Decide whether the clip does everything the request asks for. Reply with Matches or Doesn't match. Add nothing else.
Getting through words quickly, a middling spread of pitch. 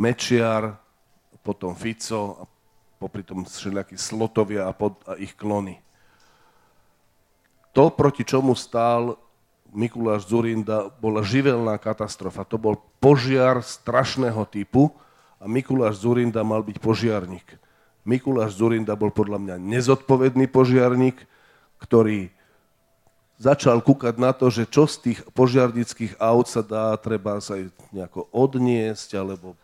Doesn't match